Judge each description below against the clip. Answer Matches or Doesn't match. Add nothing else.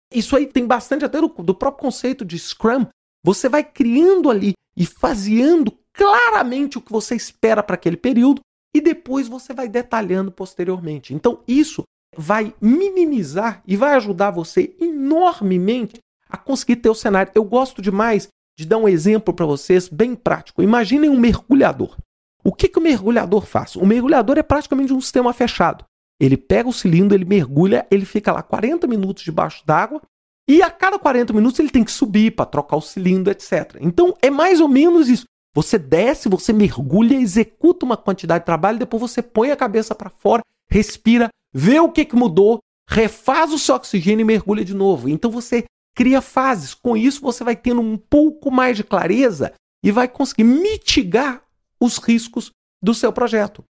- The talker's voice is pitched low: Doesn't match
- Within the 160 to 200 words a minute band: Matches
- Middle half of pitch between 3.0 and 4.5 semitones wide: Doesn't match